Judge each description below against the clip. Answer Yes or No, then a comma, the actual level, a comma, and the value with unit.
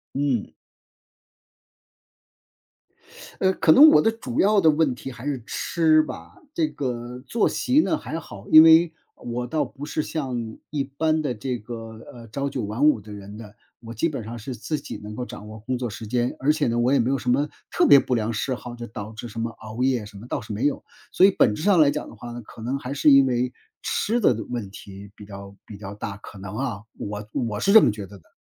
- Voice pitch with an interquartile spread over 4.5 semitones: Yes, average, 5.2 semitones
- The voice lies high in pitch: No, low, 125 Hz